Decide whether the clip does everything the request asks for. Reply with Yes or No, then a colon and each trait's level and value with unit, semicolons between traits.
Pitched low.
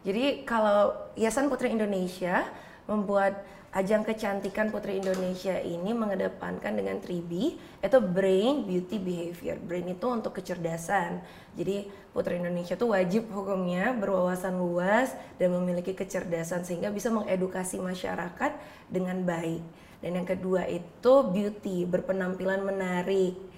No: high, 190 Hz